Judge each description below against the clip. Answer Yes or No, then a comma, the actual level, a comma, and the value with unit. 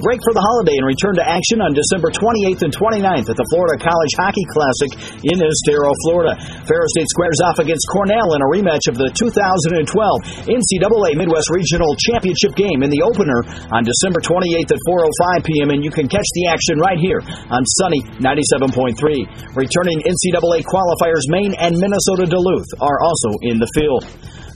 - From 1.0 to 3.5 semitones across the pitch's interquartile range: No, average, 4.2 semitones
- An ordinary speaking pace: Yes, average, 175 wpm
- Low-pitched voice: No, medium, 170 Hz